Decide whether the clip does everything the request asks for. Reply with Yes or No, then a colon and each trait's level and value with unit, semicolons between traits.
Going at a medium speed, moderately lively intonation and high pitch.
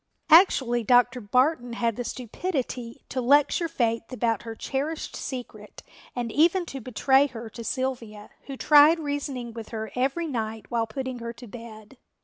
Yes: average, 155 wpm; average, 3.2 semitones; very high, 250 Hz